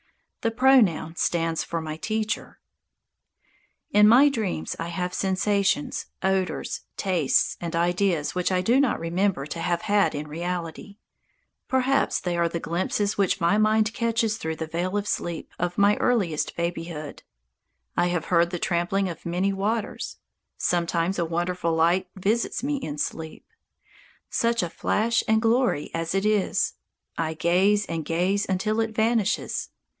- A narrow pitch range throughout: No, average, 4.1 semitones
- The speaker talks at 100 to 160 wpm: Yes, average, 150 wpm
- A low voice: No, medium, 185 Hz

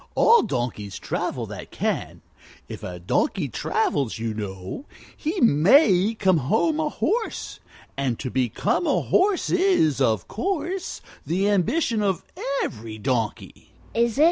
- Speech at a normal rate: No, slow, 125 wpm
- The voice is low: No, medium, 180 Hz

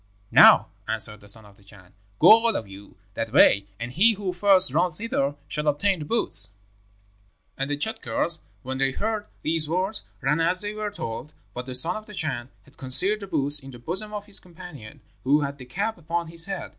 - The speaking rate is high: Yes, fast, 210 wpm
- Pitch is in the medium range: Yes, medium, 155 Hz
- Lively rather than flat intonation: Yes, wide, 7.3 semitones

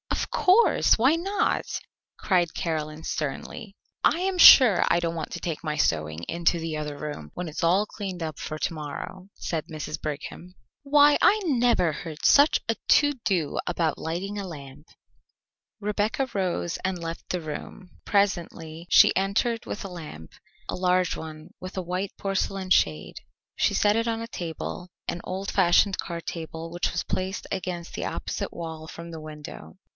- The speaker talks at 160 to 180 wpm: Yes, average, 170 wpm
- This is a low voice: No, medium, 175 Hz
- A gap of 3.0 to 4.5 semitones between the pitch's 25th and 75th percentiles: Yes, average, 3.9 semitones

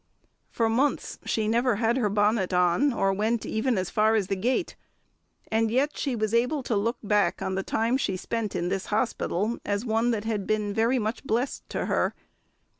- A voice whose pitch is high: Yes, high, 220 Hz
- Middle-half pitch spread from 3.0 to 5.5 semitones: No, narrow, 2.6 semitones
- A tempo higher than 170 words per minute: Yes, average, 195 wpm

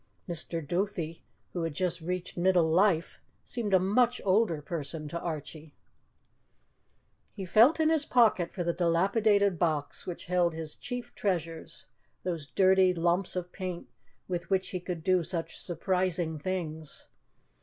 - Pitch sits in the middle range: Yes, medium, 180 Hz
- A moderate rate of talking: Yes, average, 145 wpm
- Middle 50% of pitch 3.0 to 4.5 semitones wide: No, narrow, 2.5 semitones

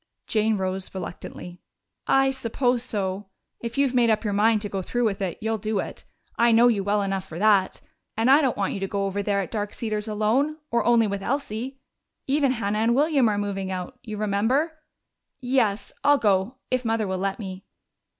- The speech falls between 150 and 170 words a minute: No, average, 195 wpm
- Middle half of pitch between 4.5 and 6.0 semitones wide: No, average, 3.5 semitones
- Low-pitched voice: No, high, 215 Hz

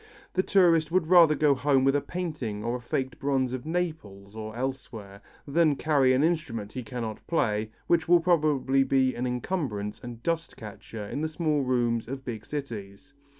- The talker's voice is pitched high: No, low, 135 Hz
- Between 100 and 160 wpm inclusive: No, average, 175 wpm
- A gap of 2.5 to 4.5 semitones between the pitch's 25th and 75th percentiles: No, wide, 5.4 semitones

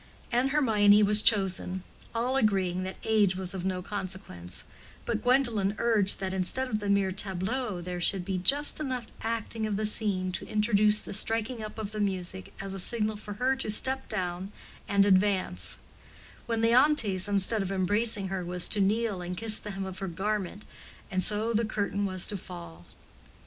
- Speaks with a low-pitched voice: No, high, 205 Hz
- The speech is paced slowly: No, average, 180 wpm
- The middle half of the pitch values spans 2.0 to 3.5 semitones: Yes, average, 2.8 semitones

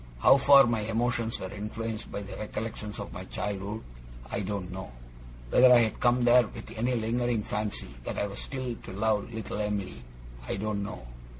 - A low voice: Yes, low, 110 Hz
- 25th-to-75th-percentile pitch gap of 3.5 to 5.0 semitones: No, average, 2.7 semitones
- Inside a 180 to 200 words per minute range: Yes, average, 185 wpm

